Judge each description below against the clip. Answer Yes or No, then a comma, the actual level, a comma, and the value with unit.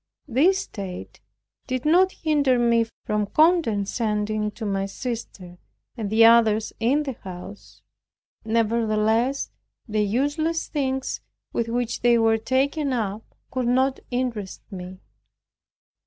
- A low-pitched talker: No, high, 230 Hz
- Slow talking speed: Yes, slow, 115 wpm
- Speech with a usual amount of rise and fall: Yes, average, 3.9 semitones